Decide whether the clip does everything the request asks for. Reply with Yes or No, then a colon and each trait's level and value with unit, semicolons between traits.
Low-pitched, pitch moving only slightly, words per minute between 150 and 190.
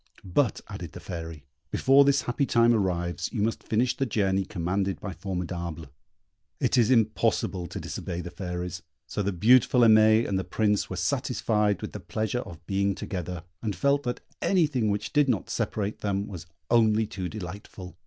No: low, 100 Hz; average, 4.4 semitones; average, 175 wpm